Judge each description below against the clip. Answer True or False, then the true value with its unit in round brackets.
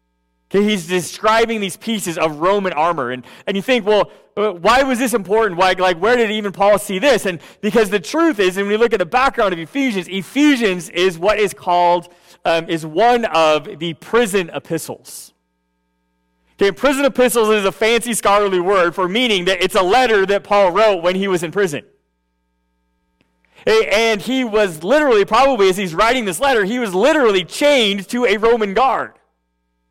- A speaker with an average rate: True (180 wpm)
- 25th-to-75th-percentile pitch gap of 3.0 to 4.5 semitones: False (4.9 semitones)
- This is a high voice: True (195 Hz)